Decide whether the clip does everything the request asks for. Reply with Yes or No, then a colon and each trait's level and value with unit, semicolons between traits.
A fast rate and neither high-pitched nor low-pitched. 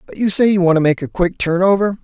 Yes: fast, 325 wpm; medium, 180 Hz